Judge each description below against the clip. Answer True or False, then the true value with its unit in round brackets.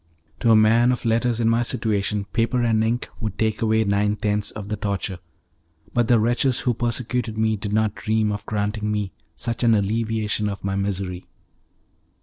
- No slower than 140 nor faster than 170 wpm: False (180 wpm)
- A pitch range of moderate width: False (2.0 semitones)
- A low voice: True (110 Hz)